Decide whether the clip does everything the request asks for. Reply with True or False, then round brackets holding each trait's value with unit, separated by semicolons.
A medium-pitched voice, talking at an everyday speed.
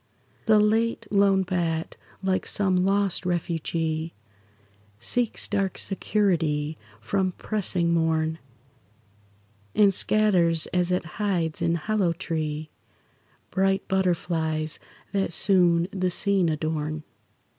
False (180 Hz; 100 wpm)